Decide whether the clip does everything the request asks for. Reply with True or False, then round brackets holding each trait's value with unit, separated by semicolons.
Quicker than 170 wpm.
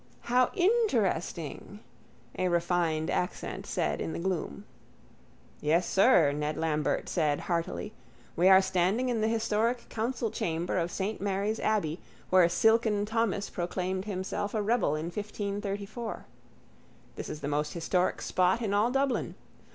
False (135 wpm)